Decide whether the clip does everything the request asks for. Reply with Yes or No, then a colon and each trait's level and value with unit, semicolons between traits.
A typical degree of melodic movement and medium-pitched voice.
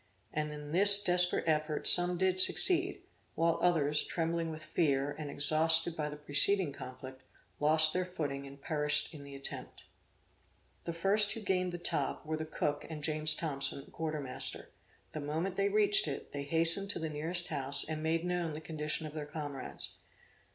Yes: average, 3.1 semitones; medium, 155 Hz